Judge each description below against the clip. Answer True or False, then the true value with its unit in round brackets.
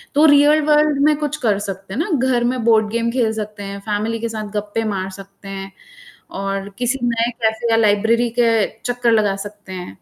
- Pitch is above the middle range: True (220 Hz)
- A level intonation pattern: False (3.2 semitones)